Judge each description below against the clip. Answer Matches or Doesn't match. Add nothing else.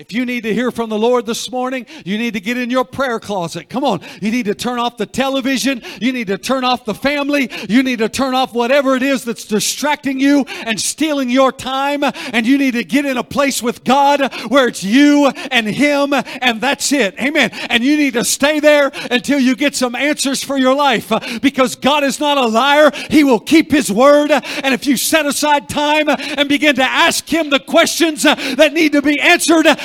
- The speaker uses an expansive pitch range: Doesn't match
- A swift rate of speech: Matches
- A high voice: Matches